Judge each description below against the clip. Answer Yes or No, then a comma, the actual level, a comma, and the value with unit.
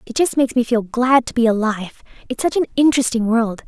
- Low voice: No, high, 240 Hz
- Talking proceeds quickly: Yes, fast, 210 wpm